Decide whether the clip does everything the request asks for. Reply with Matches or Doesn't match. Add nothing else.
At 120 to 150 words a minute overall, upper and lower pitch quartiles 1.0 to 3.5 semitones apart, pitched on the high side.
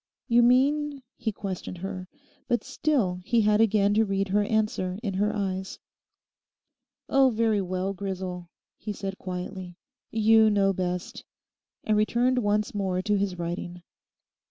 Matches